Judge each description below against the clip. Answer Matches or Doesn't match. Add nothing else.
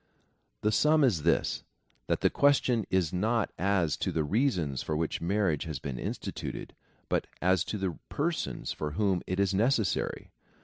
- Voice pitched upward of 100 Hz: Doesn't match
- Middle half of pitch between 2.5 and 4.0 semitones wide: Doesn't match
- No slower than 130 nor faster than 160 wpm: Doesn't match